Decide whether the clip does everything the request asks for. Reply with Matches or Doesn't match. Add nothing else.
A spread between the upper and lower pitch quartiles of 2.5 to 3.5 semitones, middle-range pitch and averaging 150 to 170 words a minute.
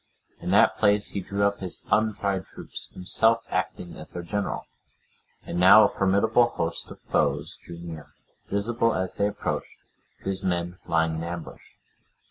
Doesn't match